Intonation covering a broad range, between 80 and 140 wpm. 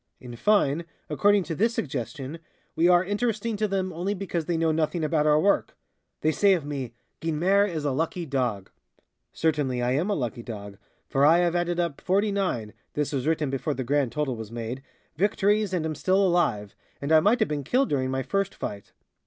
No: wide, 5.9 semitones; average, 200 wpm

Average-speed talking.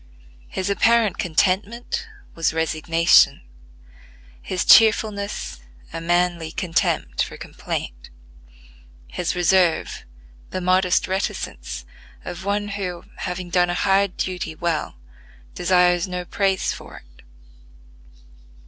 No: slow, 100 wpm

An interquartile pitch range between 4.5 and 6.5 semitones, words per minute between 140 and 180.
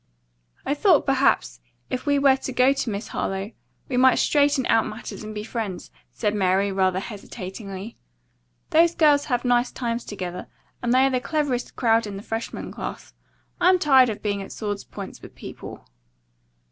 Yes: average, 4.9 semitones; average, 170 wpm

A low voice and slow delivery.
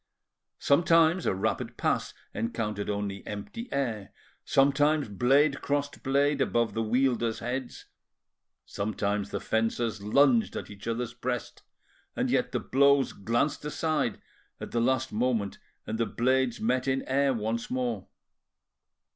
Yes: low, 120 Hz; slow, 130 wpm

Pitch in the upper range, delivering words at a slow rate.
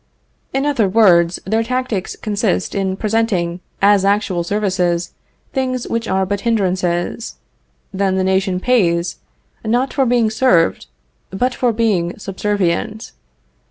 Yes: high, 200 Hz; slow, 125 wpm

